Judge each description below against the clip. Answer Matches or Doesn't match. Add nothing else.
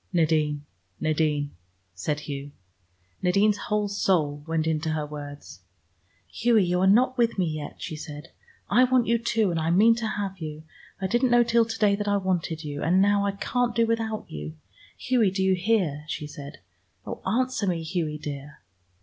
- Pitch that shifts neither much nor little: Doesn't match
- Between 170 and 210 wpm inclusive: Matches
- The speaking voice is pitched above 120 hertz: Matches